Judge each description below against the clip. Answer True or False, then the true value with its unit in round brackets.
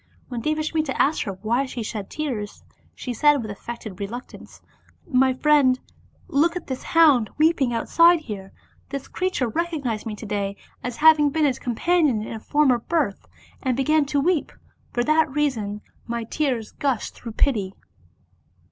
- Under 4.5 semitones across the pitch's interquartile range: False (5.2 semitones)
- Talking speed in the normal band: True (155 wpm)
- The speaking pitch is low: False (260 Hz)